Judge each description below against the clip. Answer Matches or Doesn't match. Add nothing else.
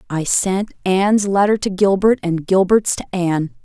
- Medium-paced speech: Matches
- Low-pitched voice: Doesn't match